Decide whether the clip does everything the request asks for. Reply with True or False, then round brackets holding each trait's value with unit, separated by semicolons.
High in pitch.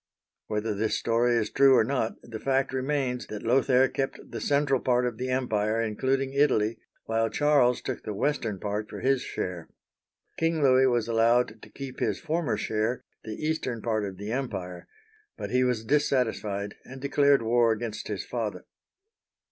False (120 Hz)